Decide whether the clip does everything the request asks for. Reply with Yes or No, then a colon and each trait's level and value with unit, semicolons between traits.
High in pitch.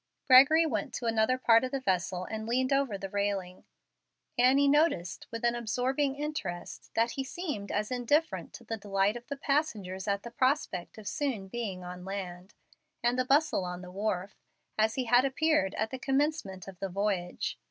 Yes: high, 225 Hz